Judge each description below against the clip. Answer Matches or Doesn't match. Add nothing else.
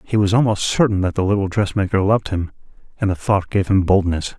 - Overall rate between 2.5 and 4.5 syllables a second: Doesn't match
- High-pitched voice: Doesn't match